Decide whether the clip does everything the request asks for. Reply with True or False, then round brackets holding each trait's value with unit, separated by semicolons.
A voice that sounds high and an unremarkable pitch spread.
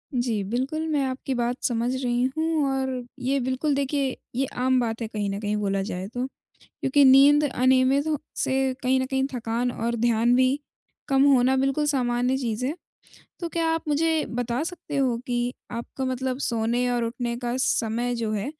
False (255 Hz; 2.3 semitones)